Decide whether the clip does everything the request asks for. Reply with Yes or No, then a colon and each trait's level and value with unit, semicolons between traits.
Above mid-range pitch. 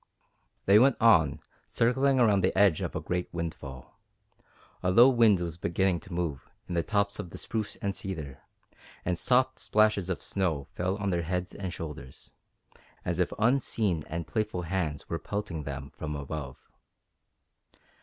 No: very low, 90 Hz